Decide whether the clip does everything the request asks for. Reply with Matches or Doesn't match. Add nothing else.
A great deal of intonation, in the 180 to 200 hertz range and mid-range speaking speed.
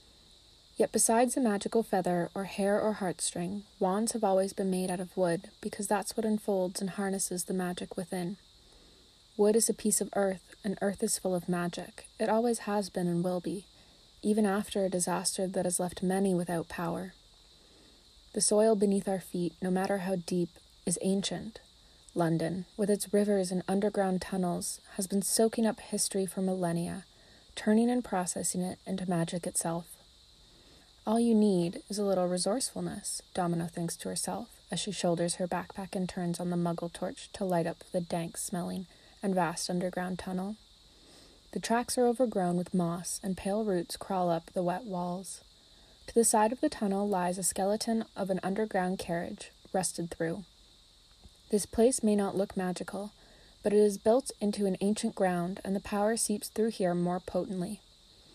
Doesn't match